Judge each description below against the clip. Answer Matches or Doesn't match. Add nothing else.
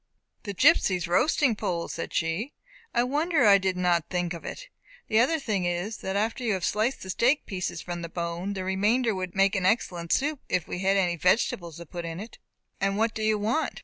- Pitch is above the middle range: Matches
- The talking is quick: Matches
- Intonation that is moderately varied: Matches